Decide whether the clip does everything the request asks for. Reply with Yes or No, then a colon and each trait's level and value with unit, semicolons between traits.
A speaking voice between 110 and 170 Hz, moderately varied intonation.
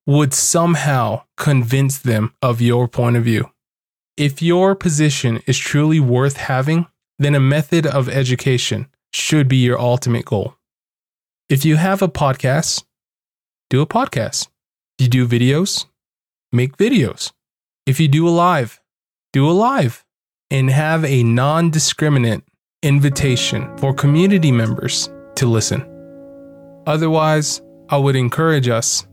Yes: medium, 140 Hz; average, 4.2 semitones